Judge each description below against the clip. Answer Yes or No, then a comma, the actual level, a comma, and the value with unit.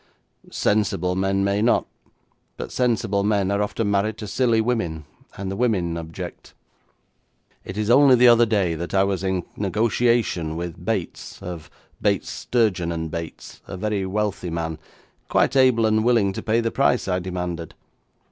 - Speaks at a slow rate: No, average, 160 wpm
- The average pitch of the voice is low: Yes, low, 100 Hz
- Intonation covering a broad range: No, average, 4.1 semitones